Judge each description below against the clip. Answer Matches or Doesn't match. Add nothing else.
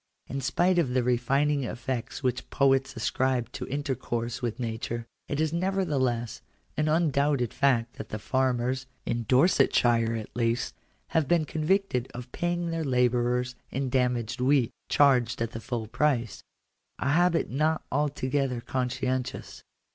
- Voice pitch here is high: Doesn't match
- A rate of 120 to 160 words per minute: Matches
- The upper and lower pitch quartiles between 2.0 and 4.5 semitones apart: Matches